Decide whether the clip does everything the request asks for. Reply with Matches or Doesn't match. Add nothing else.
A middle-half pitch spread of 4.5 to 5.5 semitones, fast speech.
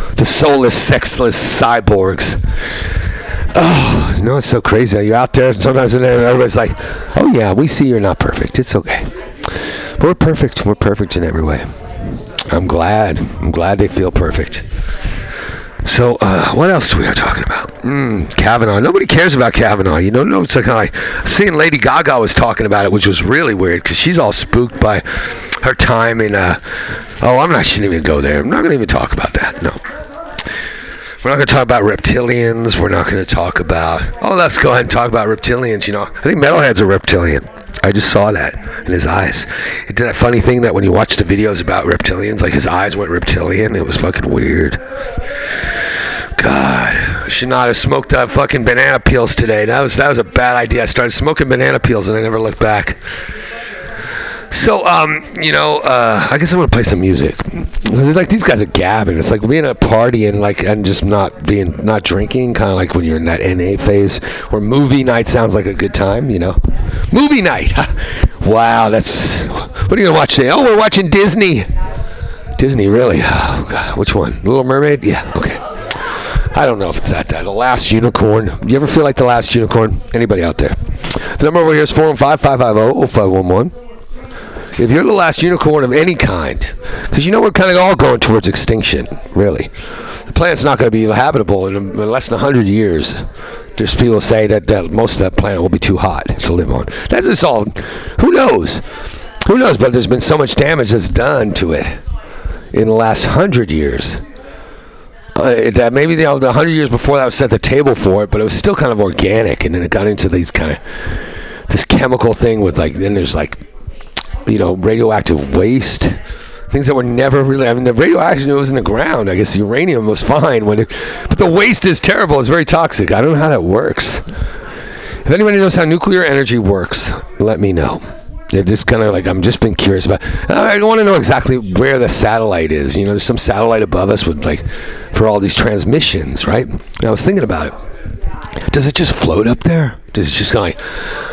Matches